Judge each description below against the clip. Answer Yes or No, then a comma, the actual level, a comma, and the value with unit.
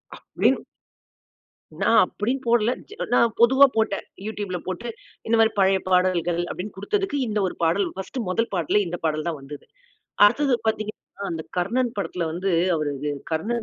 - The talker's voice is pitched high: Yes, high, 200 Hz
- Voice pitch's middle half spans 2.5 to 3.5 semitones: No, average, 4.9 semitones